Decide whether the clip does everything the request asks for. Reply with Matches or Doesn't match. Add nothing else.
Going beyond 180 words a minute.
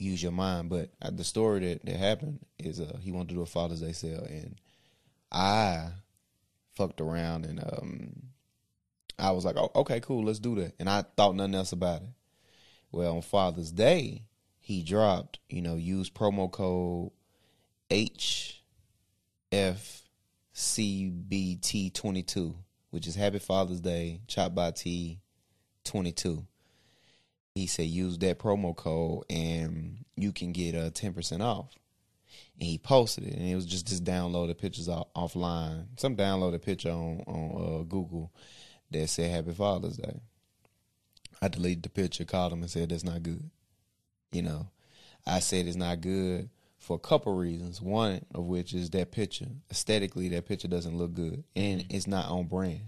Doesn't match